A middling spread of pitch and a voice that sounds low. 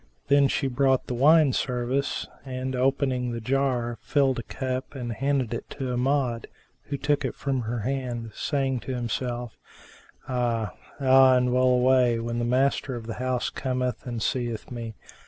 No: narrow, 2.0 semitones; low, 125 Hz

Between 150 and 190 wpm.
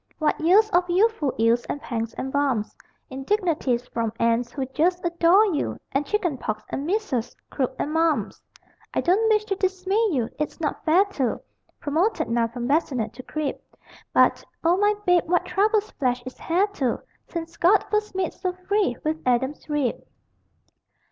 Yes: average, 170 wpm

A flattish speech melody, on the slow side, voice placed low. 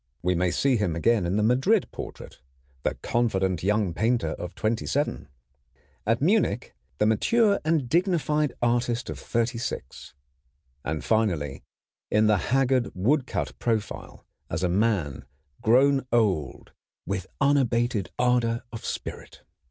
No: wide, 5.4 semitones; slow, 130 wpm; low, 115 Hz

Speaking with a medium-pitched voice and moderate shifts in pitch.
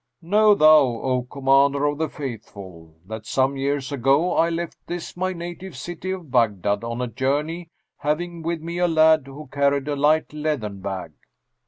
Yes: medium, 145 Hz; average, 4.5 semitones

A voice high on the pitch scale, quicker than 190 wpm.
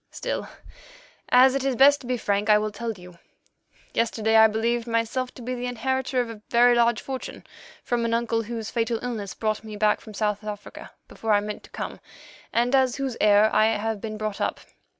Yes: high, 230 Hz; fast, 205 wpm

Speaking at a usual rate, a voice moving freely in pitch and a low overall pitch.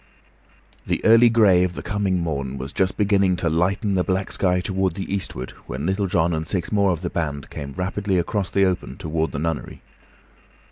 No: average, 195 wpm; average, 3.3 semitones; very low, 90 Hz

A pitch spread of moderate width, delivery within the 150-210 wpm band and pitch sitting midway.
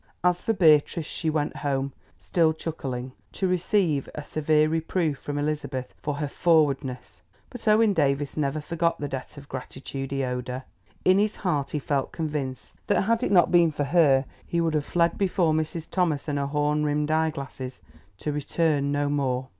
Yes: average, 3.2 semitones; average, 180 wpm; medium, 150 Hz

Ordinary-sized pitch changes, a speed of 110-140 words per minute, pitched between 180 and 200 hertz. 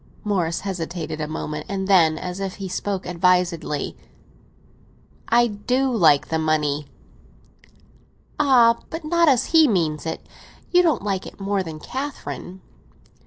No: wide, 6.3 semitones; slow, 135 wpm; high, 190 Hz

